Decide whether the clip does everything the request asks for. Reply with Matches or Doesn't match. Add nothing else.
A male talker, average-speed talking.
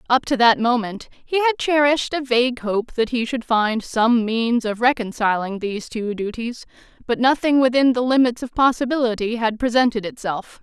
Doesn't match